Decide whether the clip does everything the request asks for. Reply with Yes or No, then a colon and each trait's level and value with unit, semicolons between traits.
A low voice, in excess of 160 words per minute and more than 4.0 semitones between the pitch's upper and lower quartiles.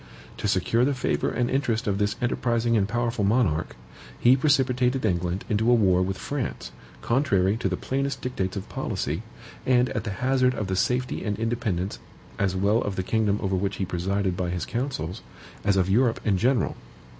Yes: low, 110 Hz; average, 185 wpm; average, 4.5 semitones